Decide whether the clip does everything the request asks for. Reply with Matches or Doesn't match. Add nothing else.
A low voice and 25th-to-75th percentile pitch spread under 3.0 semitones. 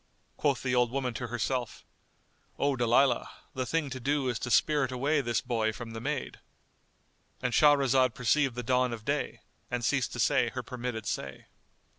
Matches